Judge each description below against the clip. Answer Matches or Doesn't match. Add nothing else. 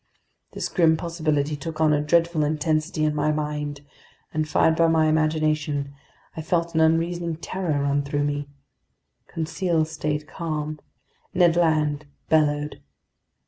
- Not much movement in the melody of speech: Matches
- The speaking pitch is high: Doesn't match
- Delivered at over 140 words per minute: Doesn't match